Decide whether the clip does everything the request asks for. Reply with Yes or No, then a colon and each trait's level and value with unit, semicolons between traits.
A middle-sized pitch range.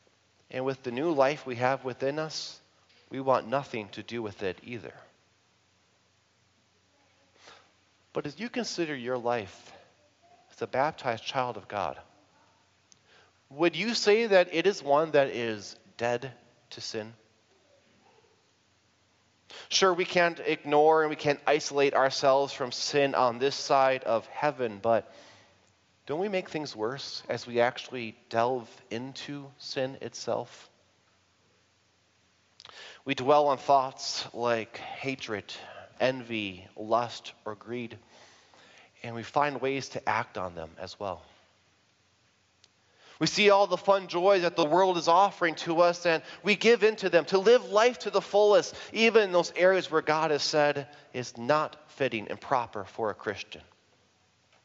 No: wide, 6.3 semitones